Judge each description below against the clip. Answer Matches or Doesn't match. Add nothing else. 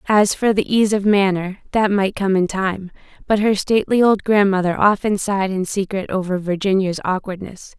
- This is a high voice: Matches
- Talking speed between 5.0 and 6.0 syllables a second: Matches